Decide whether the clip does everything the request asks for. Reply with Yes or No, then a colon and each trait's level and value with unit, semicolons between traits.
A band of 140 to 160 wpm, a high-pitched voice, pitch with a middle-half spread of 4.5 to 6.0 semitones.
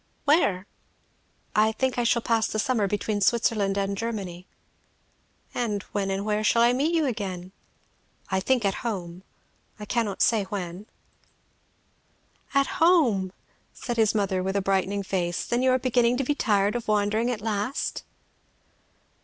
No: average, 155 wpm; high, 210 Hz; average, 3.5 semitones